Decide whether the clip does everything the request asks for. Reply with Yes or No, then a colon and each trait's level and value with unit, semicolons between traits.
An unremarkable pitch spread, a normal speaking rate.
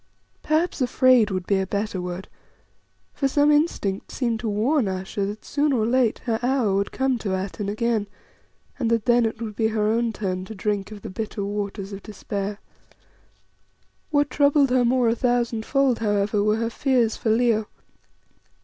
Yes: average, 3.4 semitones; average, 175 wpm